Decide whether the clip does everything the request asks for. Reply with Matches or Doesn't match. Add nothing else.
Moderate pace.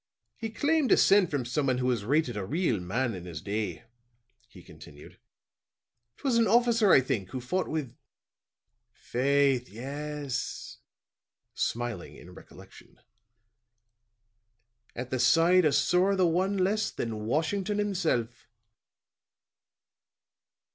Doesn't match